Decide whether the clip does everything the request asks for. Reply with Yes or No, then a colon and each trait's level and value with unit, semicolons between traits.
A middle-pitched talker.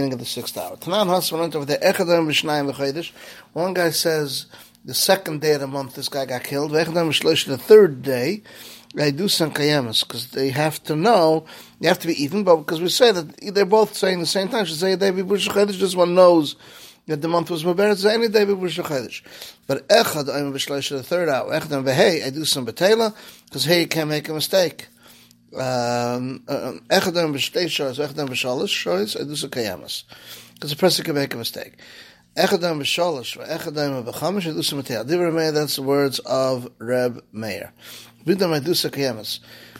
Yes: medium, 155 Hz